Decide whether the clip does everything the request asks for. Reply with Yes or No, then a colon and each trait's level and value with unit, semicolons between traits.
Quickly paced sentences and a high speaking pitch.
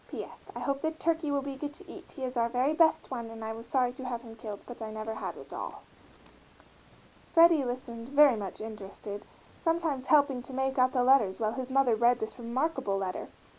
Yes: fast, 220 wpm; very high, 255 Hz